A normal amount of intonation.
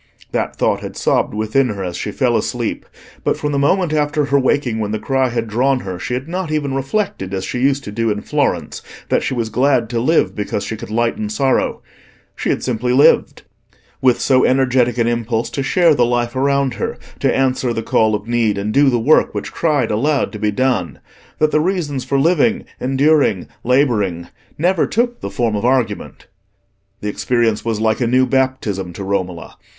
Yes: average, 4.2 semitones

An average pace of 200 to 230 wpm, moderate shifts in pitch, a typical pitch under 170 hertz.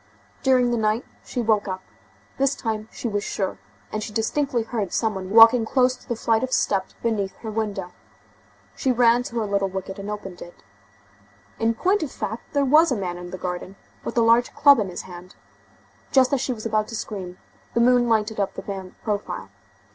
No: fast, 205 wpm; average, 3.6 semitones; high, 220 Hz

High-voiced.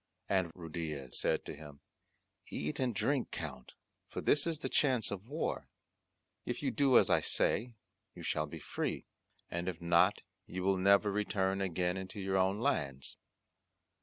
No: very low, 95 Hz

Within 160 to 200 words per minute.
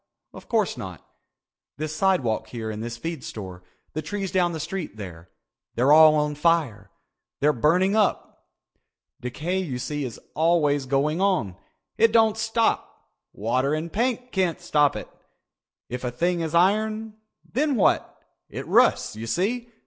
No: average, 150 wpm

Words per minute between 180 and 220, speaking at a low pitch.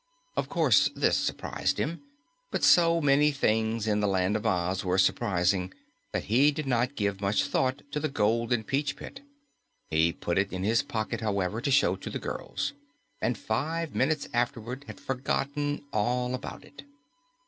No: average, 170 wpm; low, 120 Hz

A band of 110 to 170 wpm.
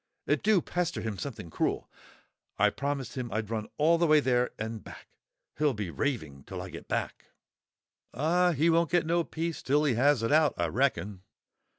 No: average, 190 wpm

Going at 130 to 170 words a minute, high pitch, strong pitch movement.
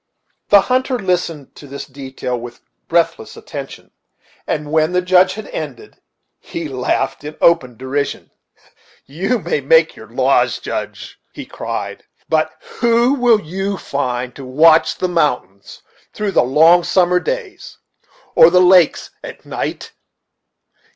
No: slow, 135 wpm; medium, 170 Hz; wide, 5.7 semitones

